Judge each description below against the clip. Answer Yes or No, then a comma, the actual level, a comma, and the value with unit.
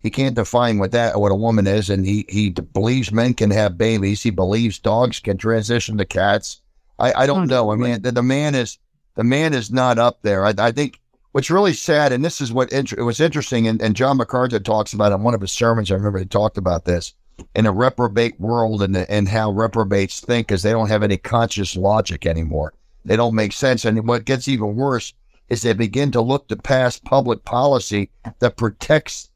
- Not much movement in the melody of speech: No, average, 3.4 semitones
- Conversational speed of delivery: No, fast, 220 wpm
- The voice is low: Yes, low, 115 Hz